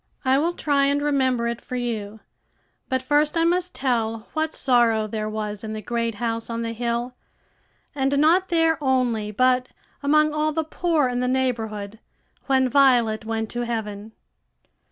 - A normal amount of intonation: Yes, average, 4.2 semitones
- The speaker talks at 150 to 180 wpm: Yes, average, 165 wpm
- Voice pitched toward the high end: Yes, very high, 250 Hz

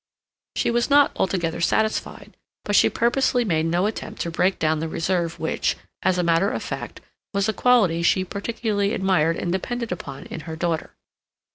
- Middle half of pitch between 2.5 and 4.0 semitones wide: No, average, 4.7 semitones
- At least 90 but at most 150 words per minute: No, average, 175 wpm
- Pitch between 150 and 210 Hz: Yes, medium, 185 Hz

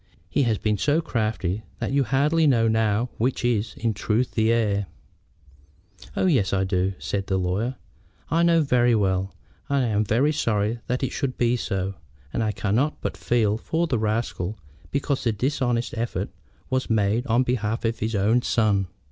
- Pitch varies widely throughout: No, average, 3.5 semitones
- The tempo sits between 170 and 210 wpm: Yes, average, 175 wpm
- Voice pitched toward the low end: Yes, low, 115 Hz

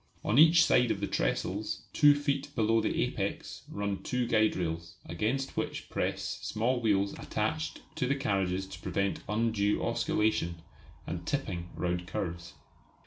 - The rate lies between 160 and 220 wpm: No, average, 145 wpm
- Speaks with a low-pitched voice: Yes, low, 105 Hz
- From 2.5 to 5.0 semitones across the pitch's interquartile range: No, wide, 5.5 semitones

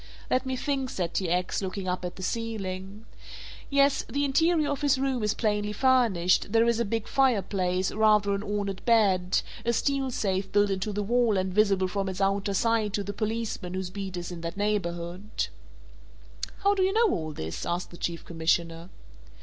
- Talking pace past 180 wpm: Yes, average, 190 wpm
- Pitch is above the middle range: Yes, high, 205 Hz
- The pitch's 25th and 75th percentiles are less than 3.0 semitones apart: No, average, 4.2 semitones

